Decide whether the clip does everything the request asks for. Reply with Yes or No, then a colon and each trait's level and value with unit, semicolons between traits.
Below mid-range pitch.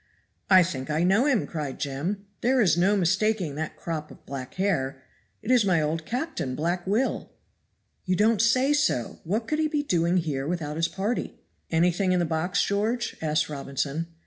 No: medium, 180 Hz